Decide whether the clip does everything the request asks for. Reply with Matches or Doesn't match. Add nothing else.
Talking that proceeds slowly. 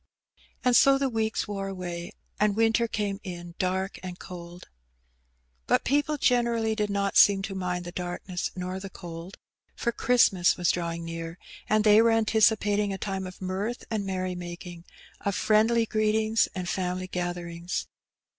Doesn't match